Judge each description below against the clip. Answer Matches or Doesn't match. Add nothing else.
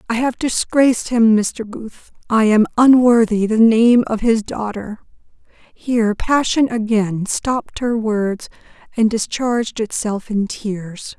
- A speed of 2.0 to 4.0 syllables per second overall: Matches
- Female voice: Matches